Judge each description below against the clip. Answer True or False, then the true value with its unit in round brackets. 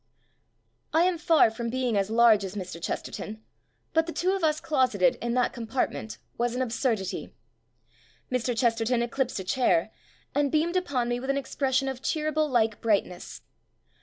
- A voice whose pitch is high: True (245 Hz)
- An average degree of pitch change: True (4.0 semitones)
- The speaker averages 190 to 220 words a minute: False (165 wpm)